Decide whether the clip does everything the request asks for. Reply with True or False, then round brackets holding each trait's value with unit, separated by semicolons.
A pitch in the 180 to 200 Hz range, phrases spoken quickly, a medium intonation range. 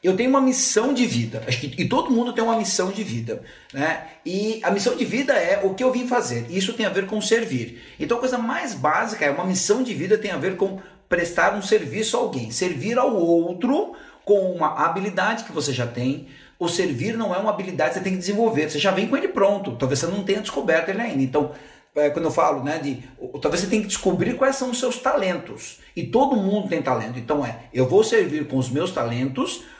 False (190 Hz; 230 wpm; 7.2 semitones)